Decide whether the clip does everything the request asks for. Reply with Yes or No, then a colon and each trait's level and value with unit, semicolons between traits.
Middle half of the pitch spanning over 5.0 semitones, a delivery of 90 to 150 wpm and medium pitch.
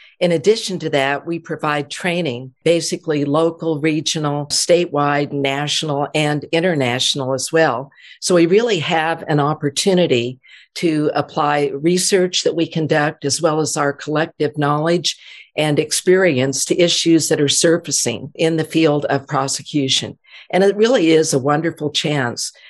No: average, 2.7 semitones; average, 140 wpm; medium, 155 Hz